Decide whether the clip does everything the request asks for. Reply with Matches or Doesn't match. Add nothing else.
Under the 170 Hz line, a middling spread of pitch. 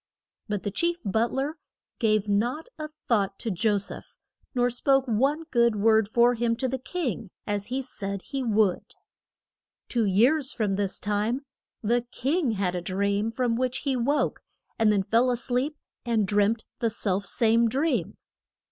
Doesn't match